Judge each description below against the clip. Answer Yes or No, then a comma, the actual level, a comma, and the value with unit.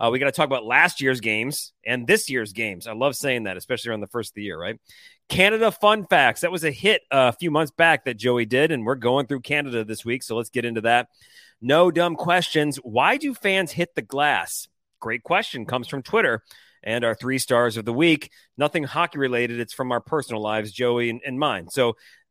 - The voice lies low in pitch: Yes, low, 130 Hz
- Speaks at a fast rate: Yes, fast, 230 wpm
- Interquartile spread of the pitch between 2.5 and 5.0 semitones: No, wide, 5.5 semitones